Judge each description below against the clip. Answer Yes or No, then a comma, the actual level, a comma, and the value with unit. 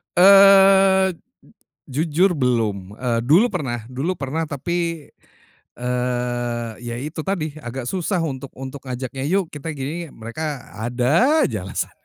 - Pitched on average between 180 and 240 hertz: No, medium, 140 Hz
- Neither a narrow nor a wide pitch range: No, wide, 6.0 semitones